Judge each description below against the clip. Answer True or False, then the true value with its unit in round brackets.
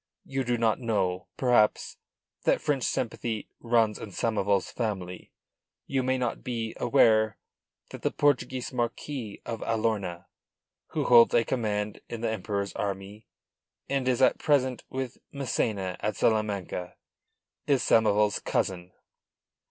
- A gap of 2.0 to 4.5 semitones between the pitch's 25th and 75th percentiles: True (3.5 semitones)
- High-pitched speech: False (115 Hz)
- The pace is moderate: False (130 wpm)